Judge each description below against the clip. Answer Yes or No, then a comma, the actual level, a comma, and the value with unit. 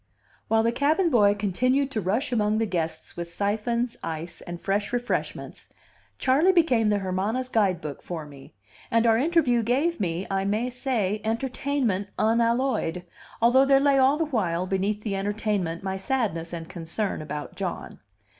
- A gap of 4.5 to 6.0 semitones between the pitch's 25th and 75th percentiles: Yes, average, 5.2 semitones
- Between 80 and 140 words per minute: No, average, 155 wpm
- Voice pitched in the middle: No, high, 215 Hz